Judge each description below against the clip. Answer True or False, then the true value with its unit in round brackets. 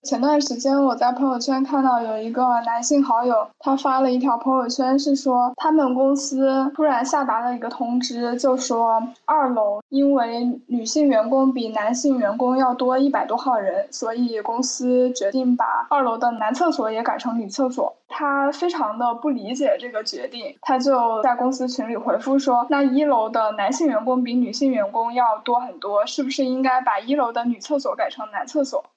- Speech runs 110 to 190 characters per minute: False (285 characters per minute)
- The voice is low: False (260 Hz)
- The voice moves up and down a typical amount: True (3.1 semitones)